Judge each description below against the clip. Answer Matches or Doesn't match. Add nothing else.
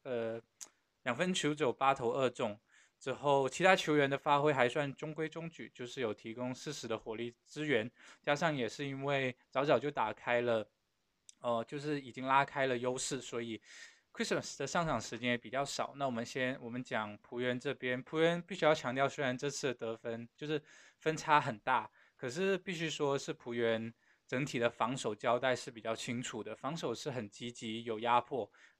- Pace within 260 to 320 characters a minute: Matches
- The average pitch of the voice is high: Doesn't match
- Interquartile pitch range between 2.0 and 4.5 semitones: Matches